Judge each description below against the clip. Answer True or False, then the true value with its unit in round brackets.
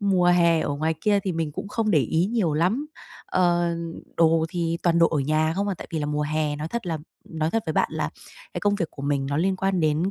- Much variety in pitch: False (3.3 semitones)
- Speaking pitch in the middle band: True (165 Hz)